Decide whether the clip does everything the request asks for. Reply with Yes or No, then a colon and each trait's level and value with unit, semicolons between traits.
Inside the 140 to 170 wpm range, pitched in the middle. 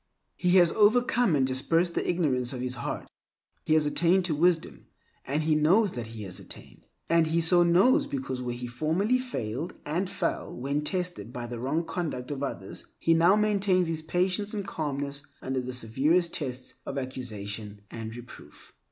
No: average, 180 wpm; medium, 155 Hz